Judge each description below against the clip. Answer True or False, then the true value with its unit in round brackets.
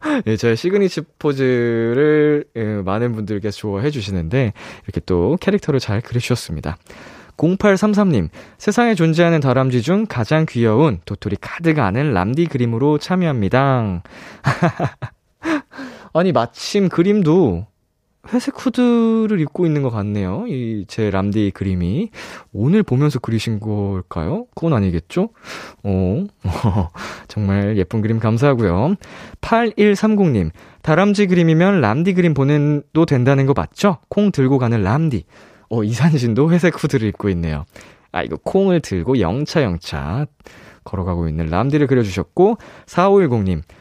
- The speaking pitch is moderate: False (130 Hz)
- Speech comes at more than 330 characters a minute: False (275 characters per minute)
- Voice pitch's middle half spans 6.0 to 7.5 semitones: False (8.9 semitones)